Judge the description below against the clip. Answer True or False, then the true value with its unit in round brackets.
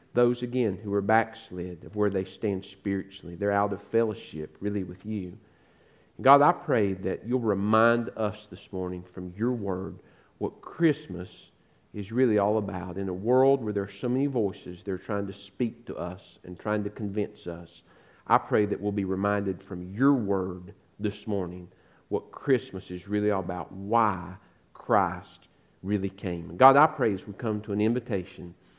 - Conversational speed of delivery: True (180 wpm)